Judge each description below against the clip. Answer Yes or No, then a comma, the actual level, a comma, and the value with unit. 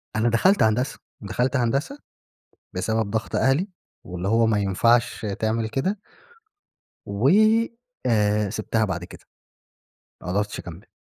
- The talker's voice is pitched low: Yes, low, 110 Hz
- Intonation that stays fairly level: No, average, 3.2 semitones